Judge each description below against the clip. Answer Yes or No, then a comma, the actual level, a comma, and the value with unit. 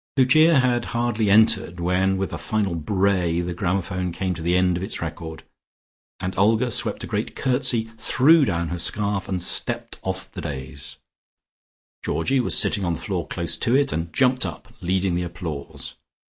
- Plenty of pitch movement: No, average, 4.6 semitones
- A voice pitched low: Yes, very low, 95 Hz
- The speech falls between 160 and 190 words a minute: Yes, average, 175 wpm